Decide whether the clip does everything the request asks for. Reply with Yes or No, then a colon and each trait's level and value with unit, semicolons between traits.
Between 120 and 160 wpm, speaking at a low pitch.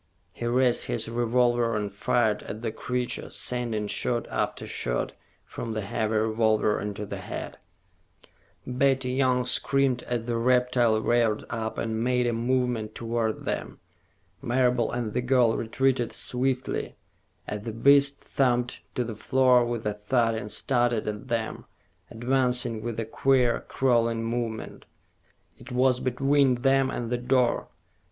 Yes: average, 145 wpm; low, 120 Hz